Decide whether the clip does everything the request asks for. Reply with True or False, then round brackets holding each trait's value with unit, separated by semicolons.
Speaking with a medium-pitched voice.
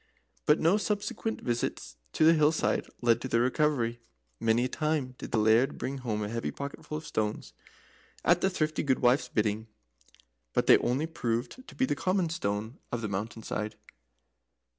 False (125 Hz)